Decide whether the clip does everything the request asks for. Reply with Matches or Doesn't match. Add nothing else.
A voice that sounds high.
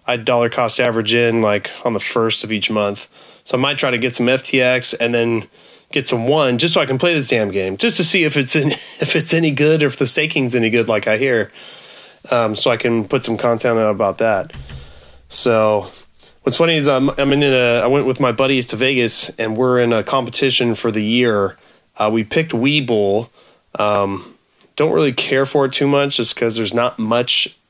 Doesn't match